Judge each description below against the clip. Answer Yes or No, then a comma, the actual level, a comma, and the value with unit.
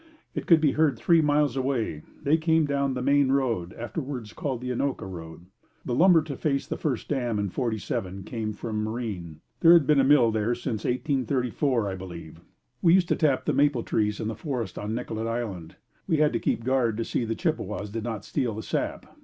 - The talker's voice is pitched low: Yes, low, 120 Hz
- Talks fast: Yes, fast, 210 wpm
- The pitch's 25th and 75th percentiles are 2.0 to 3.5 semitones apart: No, average, 4.8 semitones